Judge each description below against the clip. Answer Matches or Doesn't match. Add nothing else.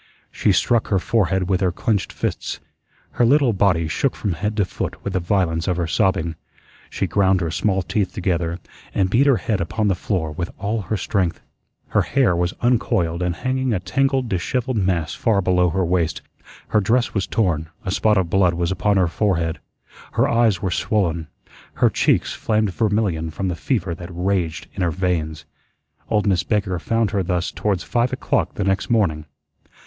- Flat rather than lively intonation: Doesn't match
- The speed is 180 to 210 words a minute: Matches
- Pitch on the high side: Doesn't match